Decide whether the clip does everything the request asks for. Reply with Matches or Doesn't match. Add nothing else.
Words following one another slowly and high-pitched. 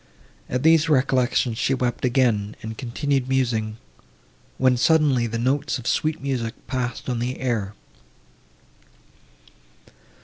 Doesn't match